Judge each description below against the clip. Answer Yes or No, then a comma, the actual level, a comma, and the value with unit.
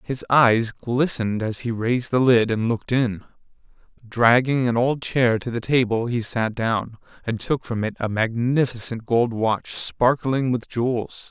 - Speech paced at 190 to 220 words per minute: No, average, 170 wpm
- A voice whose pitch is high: No, low, 120 Hz